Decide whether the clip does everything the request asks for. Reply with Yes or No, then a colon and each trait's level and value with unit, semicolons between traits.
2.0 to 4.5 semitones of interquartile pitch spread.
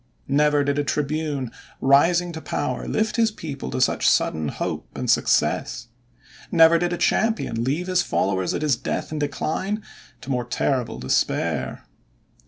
No: average, 5.0 semitones